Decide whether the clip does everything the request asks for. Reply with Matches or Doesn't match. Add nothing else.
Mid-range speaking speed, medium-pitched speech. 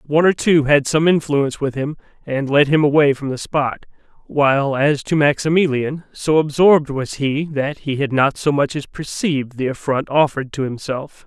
Matches